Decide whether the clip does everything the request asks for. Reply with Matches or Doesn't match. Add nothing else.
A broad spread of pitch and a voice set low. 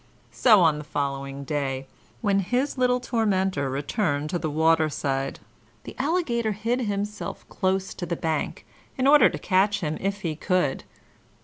Doesn't match